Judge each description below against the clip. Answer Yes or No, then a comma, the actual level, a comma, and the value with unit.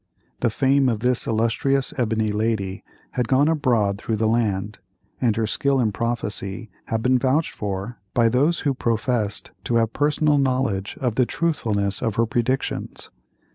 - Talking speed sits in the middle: Yes, average, 160 wpm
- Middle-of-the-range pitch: No, low, 115 Hz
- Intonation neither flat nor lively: Yes, average, 3.4 semitones